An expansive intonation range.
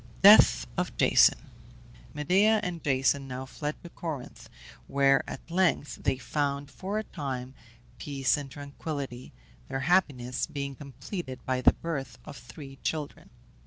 No: average, 3.6 semitones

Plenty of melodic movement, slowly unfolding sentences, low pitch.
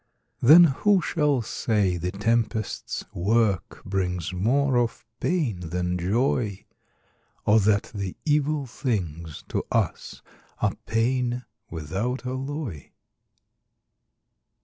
Yes: wide, 6.1 semitones; slow, 100 wpm; low, 110 Hz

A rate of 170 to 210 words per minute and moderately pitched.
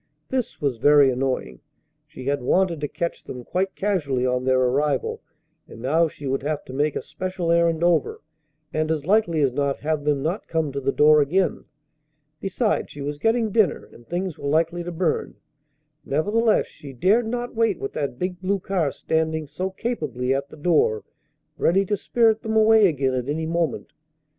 Yes: average, 185 wpm; medium, 160 Hz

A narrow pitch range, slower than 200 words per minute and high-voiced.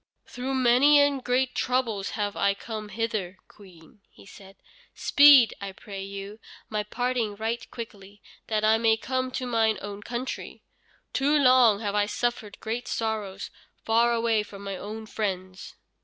No: average, 3.3 semitones; average, 155 wpm; high, 220 Hz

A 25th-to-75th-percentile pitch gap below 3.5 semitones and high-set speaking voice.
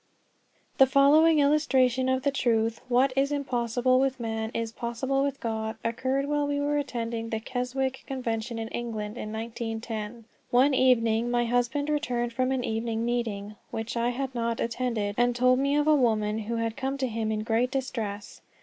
Yes: average, 2.8 semitones; high, 240 Hz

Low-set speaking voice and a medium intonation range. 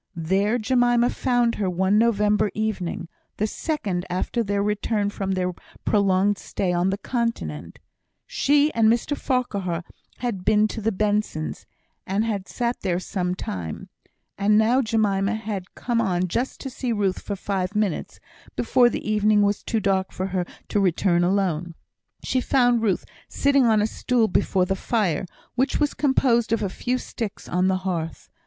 No: high, 205 Hz; average, 3.8 semitones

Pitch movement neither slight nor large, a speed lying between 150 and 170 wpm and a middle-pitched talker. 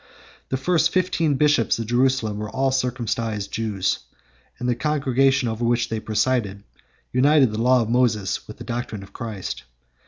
No: average, 3.4 semitones; average, 160 wpm; low, 120 Hz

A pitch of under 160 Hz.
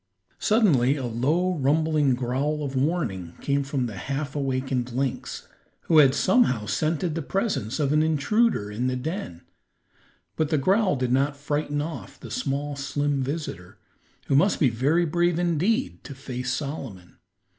Yes: medium, 140 Hz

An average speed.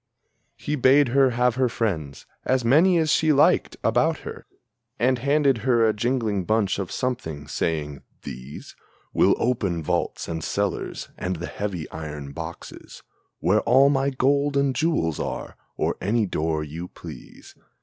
Yes: average, 150 wpm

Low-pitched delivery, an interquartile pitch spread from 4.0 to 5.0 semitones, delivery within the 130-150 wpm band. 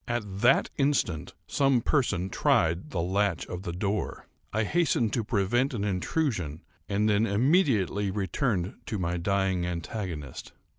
Yes: low, 100 Hz; average, 4.7 semitones; average, 140 wpm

